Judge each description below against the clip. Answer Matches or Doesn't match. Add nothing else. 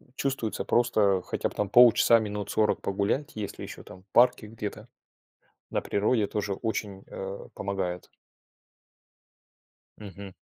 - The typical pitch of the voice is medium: Doesn't match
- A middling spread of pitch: Doesn't match